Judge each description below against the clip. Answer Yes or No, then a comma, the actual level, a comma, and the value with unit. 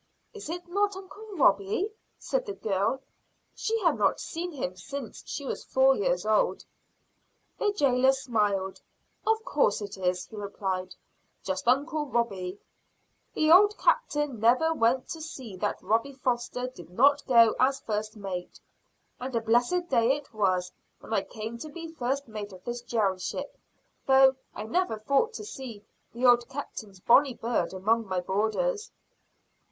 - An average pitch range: No, wide, 6.1 semitones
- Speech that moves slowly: No, average, 160 wpm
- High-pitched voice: Yes, high, 240 Hz